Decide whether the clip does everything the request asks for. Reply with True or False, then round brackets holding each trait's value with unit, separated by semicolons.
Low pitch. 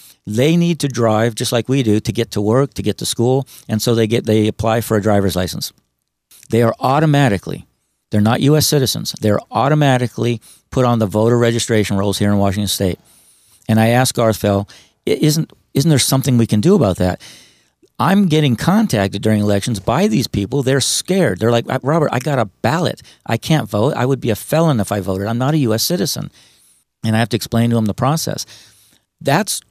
True (115 Hz)